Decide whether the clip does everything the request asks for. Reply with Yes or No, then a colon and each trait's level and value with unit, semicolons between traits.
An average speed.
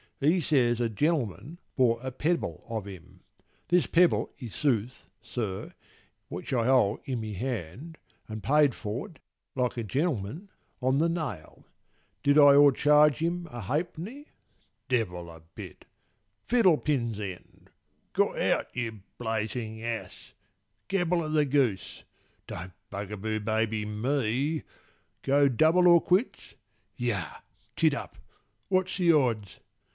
No: slow, 125 wpm